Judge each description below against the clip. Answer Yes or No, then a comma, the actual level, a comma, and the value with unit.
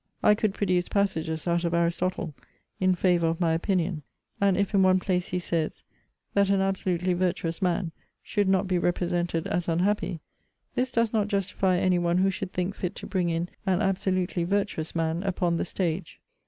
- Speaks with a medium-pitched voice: Yes, medium, 180 Hz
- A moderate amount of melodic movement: No, narrow, 2.2 semitones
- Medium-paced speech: Yes, average, 180 wpm